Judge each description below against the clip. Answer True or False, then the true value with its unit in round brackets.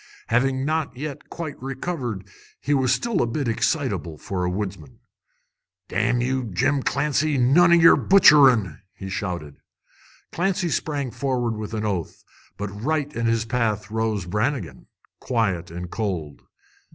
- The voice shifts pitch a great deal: True (5.8 semitones)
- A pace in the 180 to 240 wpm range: False (140 wpm)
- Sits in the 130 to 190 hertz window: False (120 Hz)